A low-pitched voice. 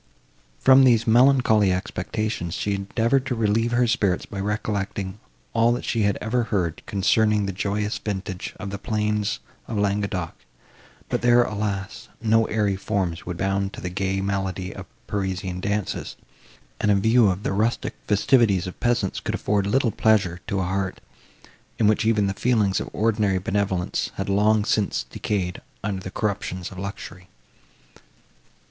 Yes: low, 100 Hz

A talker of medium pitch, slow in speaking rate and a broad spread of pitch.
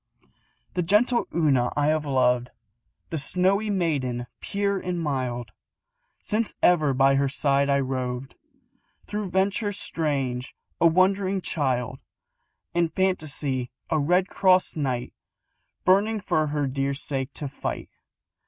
Yes: medium, 150 Hz; slow, 125 wpm; wide, 5.7 semitones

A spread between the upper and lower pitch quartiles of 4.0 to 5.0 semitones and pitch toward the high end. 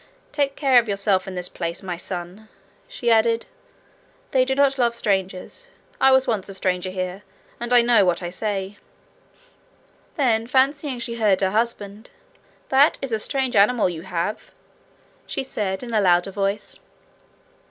Yes: average, 4.7 semitones; high, 215 Hz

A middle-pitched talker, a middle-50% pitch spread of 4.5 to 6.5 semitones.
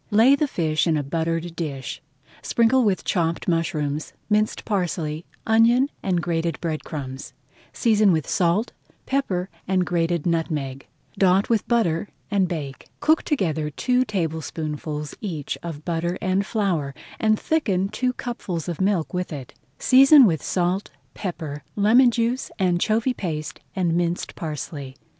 Yes: medium, 175 Hz; average, 5.2 semitones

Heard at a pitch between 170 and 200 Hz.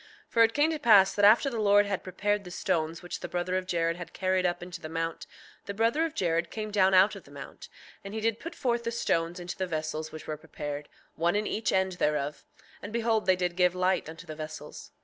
Yes: medium, 185 Hz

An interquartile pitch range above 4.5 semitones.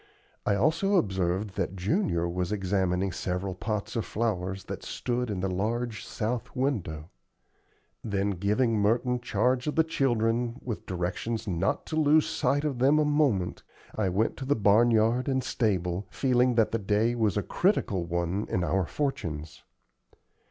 Yes: average, 4.9 semitones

